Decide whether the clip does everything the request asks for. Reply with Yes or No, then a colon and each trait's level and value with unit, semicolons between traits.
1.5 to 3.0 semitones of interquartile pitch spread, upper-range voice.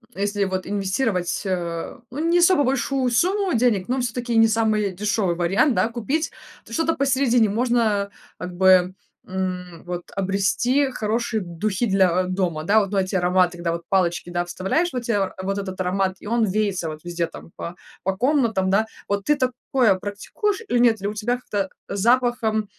No: average, 4.5 semitones; high, 205 Hz